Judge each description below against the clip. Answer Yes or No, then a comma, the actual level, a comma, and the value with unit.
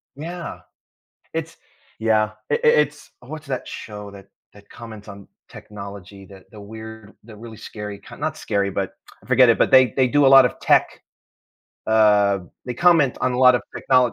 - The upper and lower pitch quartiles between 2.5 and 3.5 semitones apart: No, average, 4.0 semitones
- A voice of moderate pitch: No, low, 110 Hz